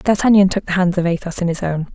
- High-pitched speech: No, medium, 180 Hz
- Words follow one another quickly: Yes, fast, 280 wpm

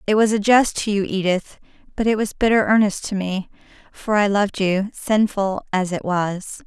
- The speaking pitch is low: No, high, 205 Hz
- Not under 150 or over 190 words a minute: No, average, 200 wpm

